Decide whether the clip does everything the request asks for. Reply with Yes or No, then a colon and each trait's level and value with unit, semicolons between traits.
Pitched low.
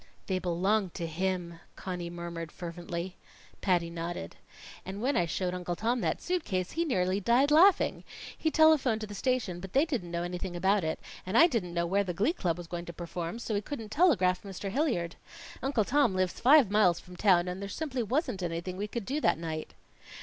No: high, 190 Hz